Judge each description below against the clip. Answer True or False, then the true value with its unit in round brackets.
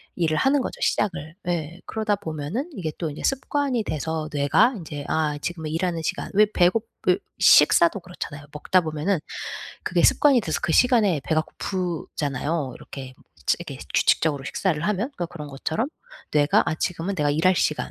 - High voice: False (165 Hz)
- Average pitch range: True (4.4 semitones)